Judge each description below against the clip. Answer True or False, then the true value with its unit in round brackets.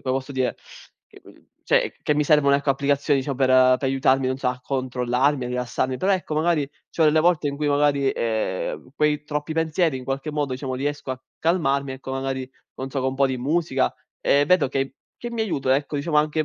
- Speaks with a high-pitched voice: False (140 Hz)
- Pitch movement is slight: True (2.3 semitones)